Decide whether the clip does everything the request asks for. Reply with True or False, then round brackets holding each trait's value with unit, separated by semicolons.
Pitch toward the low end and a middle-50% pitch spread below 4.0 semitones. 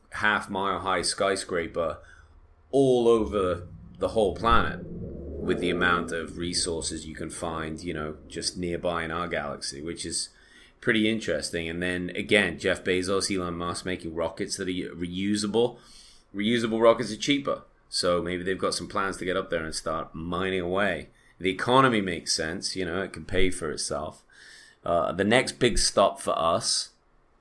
True (90 Hz; 3.3 semitones)